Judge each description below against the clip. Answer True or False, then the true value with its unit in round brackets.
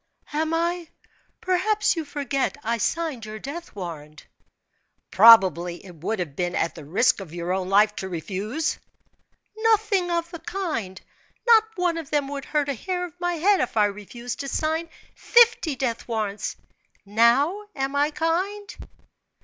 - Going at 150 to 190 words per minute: True (155 wpm)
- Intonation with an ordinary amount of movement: False (8.8 semitones)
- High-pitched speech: True (275 Hz)